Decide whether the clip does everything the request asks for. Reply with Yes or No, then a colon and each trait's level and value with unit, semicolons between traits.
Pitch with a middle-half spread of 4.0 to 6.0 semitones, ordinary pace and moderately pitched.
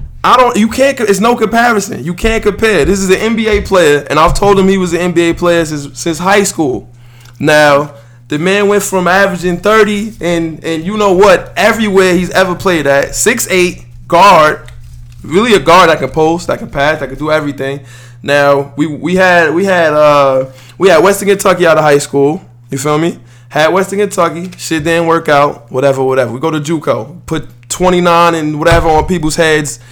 Yes: average, 5.1 semitones; average, 195 wpm; medium, 165 Hz